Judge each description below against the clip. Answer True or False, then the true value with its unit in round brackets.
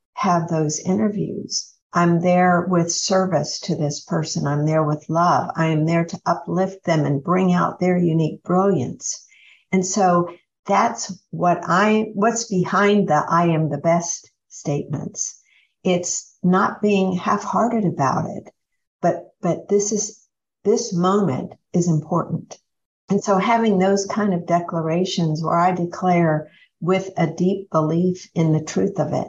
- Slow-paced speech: False (150 wpm)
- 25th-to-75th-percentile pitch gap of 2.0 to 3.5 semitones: True (2.7 semitones)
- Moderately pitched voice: True (180 Hz)